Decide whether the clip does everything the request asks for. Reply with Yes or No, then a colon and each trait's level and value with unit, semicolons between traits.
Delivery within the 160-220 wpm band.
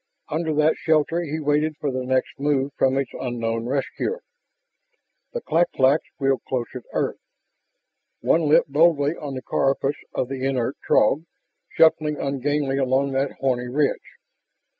No: average, 145 wpm